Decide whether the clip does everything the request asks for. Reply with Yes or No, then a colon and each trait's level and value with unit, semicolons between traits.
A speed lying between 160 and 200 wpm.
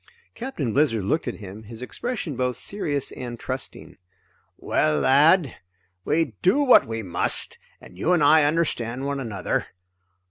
No: average, 145 wpm